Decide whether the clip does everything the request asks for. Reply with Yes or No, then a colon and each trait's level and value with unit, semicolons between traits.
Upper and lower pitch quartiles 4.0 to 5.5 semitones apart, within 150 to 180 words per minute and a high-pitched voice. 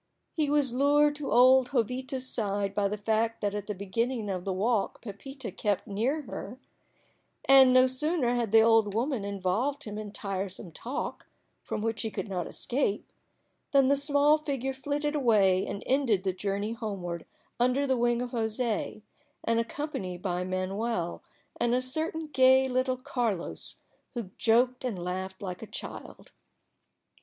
Yes: average, 4.7 semitones; average, 160 wpm; high, 230 Hz